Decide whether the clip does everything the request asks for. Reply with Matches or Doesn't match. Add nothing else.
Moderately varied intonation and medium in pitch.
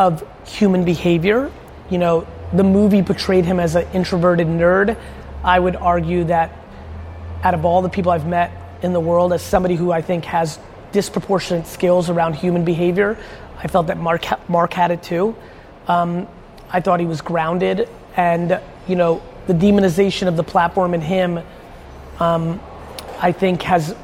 Doesn't match